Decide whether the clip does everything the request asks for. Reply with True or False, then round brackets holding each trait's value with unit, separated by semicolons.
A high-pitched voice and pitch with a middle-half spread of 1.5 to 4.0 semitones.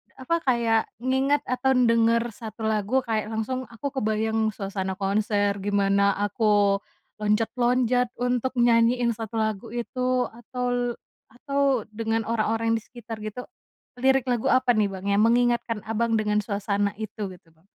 True (225 Hz; 2.8 semitones)